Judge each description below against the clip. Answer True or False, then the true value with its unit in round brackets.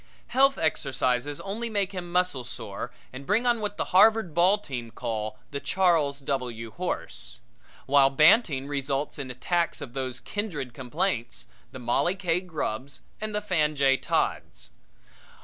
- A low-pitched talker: False (145 Hz)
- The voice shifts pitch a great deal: True (6.3 semitones)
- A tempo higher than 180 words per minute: False (150 wpm)